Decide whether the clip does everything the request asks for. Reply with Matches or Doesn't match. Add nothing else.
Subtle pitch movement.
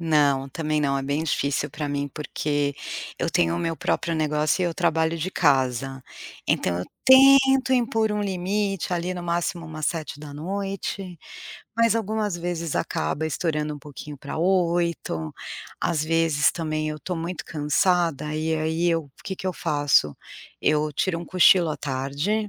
Doesn't match